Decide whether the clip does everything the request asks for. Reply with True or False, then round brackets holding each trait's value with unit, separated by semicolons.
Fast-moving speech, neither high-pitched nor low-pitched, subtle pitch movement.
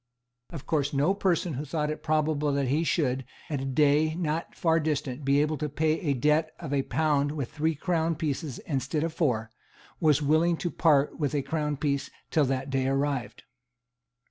False (190 wpm; 150 Hz; 2.3 semitones)